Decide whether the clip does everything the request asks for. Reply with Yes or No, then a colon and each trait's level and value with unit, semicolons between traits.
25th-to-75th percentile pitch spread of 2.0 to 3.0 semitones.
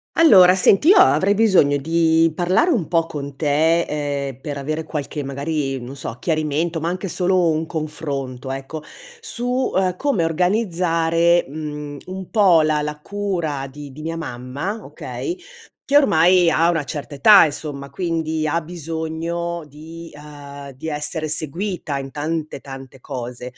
No: average, 3.5 semitones